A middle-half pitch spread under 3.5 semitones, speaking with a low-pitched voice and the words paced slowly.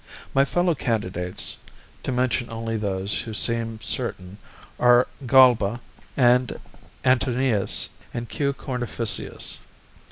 Yes: average, 2.8 semitones; low, 120 Hz; slow, 100 wpm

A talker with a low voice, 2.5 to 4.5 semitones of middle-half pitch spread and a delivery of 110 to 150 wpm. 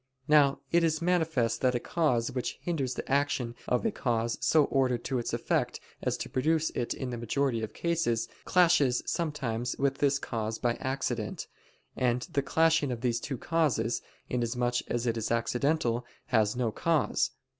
No: low, 125 Hz; average, 4.2 semitones; average, 170 wpm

